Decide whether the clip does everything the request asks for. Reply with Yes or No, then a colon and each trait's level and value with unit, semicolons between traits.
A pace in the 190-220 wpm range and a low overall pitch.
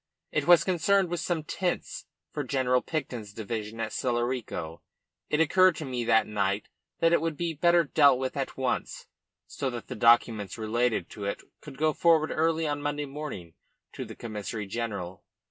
No: average, 175 wpm; low, 130 Hz